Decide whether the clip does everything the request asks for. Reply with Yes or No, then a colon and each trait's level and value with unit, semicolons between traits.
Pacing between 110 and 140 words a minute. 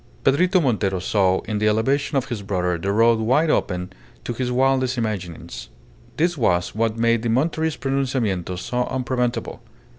No: average, 155 wpm